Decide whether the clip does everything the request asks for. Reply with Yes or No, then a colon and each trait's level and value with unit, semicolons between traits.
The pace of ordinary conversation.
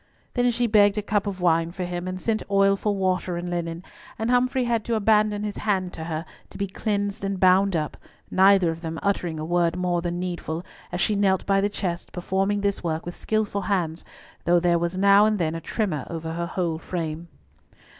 No: fast, 215 wpm